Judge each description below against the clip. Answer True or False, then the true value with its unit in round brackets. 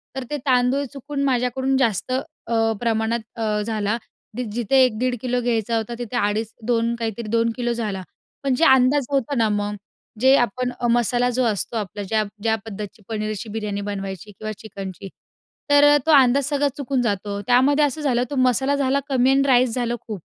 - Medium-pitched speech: False (235 Hz)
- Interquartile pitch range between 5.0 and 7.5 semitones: False (3.3 semitones)